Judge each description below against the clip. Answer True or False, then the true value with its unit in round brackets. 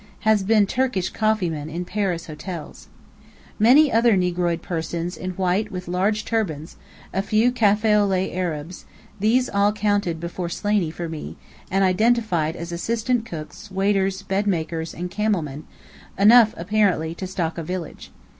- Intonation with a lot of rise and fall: False (3.8 semitones)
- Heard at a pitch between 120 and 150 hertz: False (190 Hz)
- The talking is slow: False (155 wpm)